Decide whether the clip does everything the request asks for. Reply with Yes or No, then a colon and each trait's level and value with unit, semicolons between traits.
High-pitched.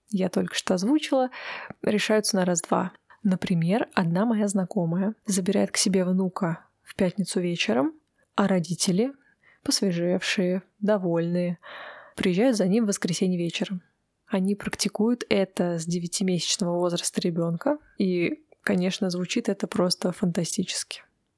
Yes: high, 195 Hz